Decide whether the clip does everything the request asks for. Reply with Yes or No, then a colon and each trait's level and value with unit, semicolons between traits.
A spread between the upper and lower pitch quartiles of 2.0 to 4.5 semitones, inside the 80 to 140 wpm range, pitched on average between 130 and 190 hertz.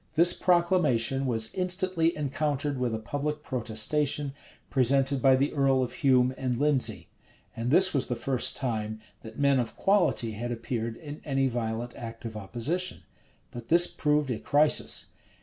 No: average, 4.1 semitones; average, 155 wpm; low, 135 Hz